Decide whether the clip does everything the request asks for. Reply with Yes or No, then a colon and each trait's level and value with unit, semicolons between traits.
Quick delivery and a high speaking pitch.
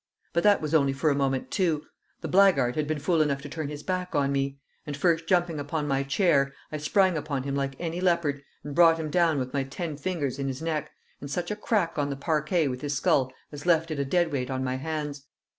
No: fast, 240 wpm; medium, 150 Hz